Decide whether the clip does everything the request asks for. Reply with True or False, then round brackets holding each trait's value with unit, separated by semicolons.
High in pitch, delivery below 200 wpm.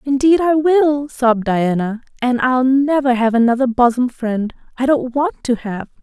True (250 Hz; 160 wpm)